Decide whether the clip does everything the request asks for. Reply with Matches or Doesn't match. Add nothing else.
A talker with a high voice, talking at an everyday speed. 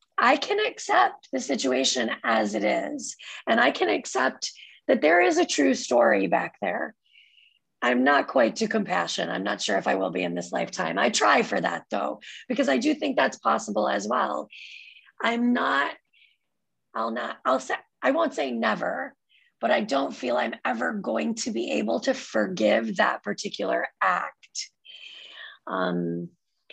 Matches